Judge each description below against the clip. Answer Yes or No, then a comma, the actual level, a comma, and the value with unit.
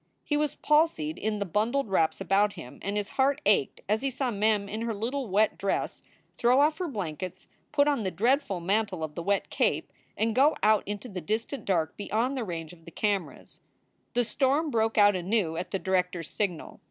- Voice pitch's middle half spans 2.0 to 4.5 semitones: No, average, 5.0 semitones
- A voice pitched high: Yes, high, 210 Hz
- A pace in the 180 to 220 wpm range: Yes, fast, 205 wpm